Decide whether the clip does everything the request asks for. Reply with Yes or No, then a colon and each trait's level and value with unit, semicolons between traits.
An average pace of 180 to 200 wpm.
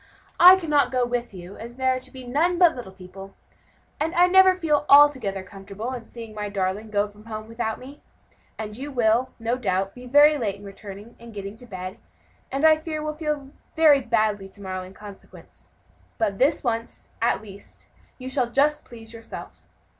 Yes: average, 190 wpm